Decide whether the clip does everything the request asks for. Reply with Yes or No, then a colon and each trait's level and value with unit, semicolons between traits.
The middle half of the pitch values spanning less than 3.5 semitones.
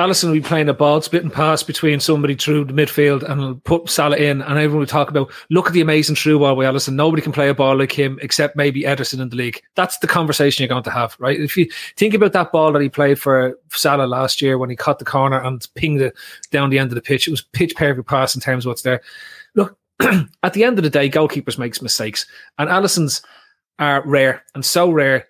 Yes: average, 2.7 semitones